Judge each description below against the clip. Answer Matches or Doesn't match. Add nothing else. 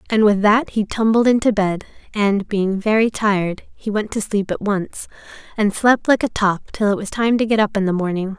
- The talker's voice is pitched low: Doesn't match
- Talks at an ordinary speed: Doesn't match